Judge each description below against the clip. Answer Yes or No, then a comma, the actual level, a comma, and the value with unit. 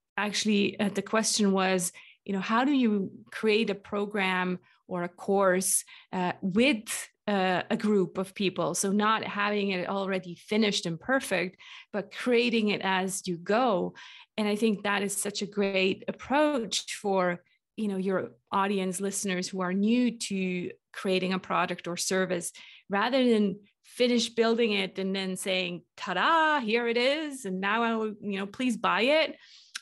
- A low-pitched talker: No, high, 200 Hz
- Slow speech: No, average, 165 wpm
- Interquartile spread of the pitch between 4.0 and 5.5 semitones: No, average, 2.9 semitones